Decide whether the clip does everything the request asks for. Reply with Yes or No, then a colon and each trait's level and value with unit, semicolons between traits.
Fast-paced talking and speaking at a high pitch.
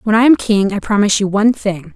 Yes: fast, 275 wpm; high, 210 Hz